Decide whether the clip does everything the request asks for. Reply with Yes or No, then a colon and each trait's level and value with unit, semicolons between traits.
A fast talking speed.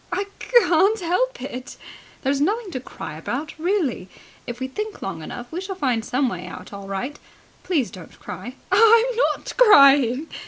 No: average, 170 wpm